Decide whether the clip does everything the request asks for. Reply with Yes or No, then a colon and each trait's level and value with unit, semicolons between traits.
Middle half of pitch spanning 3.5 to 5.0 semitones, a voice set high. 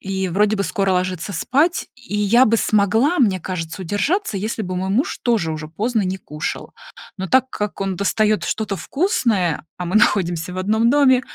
Yes: average, 4.1 semitones; high, 205 Hz